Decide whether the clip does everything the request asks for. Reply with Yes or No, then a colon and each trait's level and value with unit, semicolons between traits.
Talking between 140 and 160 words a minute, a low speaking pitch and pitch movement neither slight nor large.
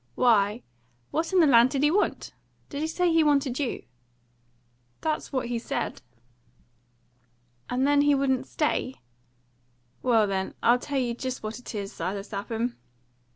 No: average, 155 wpm; very high, 255 Hz; average, 4.0 semitones